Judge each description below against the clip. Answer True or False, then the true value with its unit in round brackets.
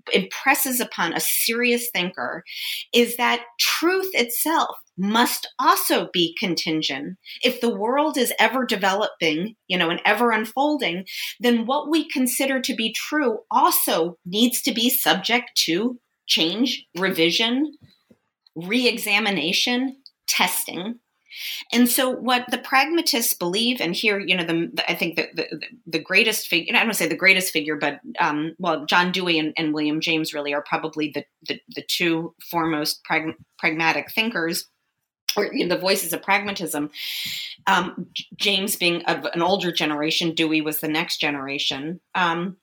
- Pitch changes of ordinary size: False (6.9 semitones)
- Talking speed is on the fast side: False (150 wpm)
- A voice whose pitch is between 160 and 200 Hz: True (190 Hz)